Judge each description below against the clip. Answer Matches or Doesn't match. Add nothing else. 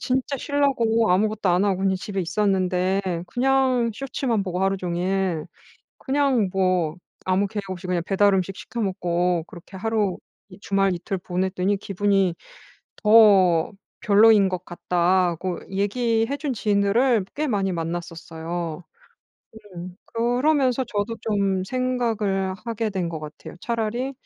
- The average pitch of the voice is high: Matches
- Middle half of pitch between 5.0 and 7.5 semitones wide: Doesn't match